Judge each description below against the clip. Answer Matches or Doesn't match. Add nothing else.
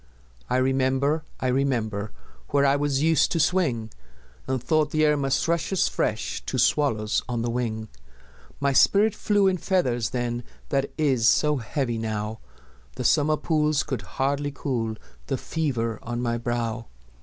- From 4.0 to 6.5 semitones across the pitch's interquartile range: Matches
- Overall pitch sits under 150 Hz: Matches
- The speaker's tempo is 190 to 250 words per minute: Doesn't match